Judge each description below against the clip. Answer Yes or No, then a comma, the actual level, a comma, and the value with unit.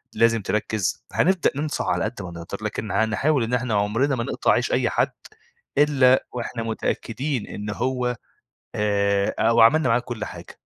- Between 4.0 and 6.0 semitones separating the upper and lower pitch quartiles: No, average, 3.5 semitones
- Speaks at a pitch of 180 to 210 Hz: No, low, 115 Hz